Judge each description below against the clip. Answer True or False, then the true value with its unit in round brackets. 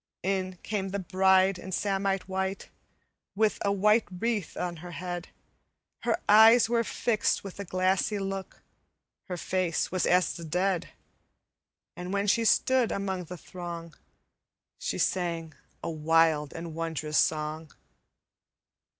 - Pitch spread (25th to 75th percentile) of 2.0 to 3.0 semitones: True (2.7 semitones)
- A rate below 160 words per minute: True (135 wpm)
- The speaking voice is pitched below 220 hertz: True (185 Hz)